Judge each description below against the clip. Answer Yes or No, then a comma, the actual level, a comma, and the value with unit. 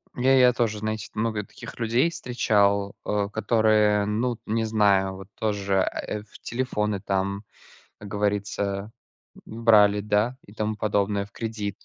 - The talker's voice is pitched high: No, low, 105 Hz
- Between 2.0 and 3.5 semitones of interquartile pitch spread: No, narrow, 1.6 semitones